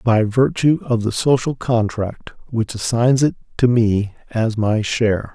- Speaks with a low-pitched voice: Yes, low, 115 Hz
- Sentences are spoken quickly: No, average, 155 wpm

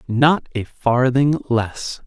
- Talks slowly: Yes, slow, 115 wpm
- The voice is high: No, low, 125 Hz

